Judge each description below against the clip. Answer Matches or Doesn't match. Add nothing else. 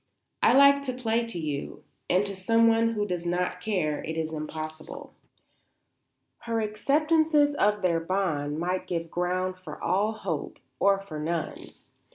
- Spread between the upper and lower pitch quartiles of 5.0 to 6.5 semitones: Matches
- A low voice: Doesn't match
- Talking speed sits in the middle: Matches